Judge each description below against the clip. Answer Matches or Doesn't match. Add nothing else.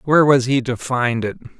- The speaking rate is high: Matches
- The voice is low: Matches